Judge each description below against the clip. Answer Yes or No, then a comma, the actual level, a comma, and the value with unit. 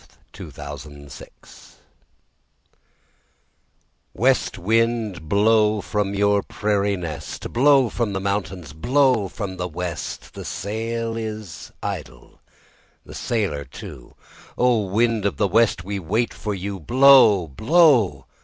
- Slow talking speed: Yes, slow, 125 wpm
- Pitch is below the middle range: Yes, low, 100 Hz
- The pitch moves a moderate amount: Yes, average, 4.2 semitones